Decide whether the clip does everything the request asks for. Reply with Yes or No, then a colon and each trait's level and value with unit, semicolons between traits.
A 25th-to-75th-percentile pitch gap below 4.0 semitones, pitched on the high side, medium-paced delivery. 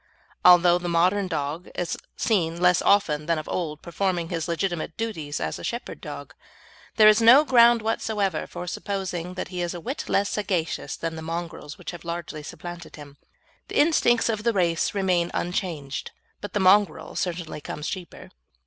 No: average, 3.4 semitones; medium, 175 Hz; average, 175 wpm